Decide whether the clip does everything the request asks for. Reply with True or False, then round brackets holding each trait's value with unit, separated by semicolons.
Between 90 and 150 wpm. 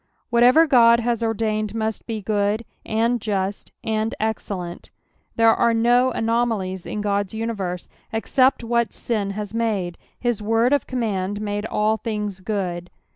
True (140 wpm)